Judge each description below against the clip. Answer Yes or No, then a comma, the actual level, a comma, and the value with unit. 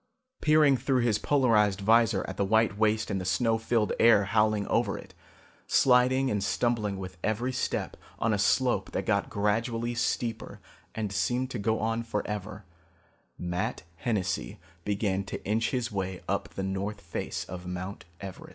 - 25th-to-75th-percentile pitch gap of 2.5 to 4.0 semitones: Yes, average, 3.1 semitones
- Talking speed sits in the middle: Yes, average, 160 wpm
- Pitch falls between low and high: No, low, 105 Hz